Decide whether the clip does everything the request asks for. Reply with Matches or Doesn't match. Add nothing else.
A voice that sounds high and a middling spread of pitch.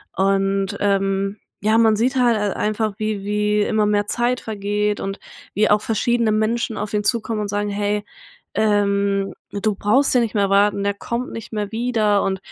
Doesn't match